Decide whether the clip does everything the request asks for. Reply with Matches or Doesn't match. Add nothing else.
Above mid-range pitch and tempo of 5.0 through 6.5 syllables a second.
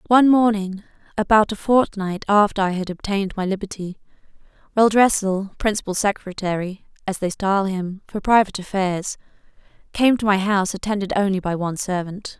Matches